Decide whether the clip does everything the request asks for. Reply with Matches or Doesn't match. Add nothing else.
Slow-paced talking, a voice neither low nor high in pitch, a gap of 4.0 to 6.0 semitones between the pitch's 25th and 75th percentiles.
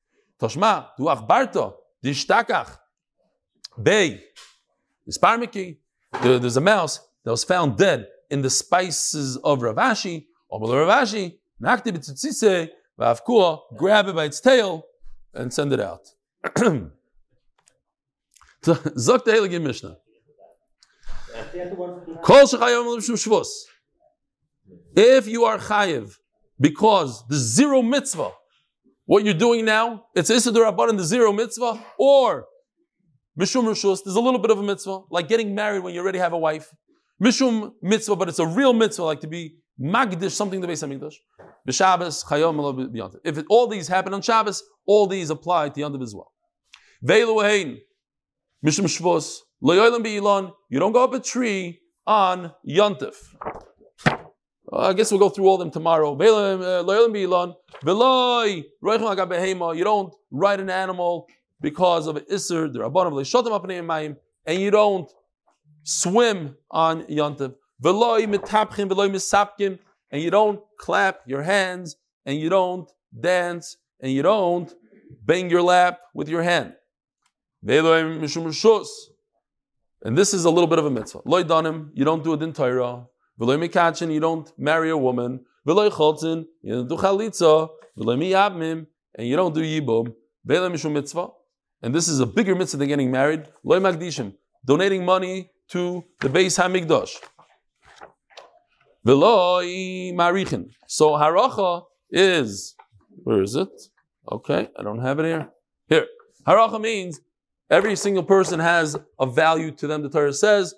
Matches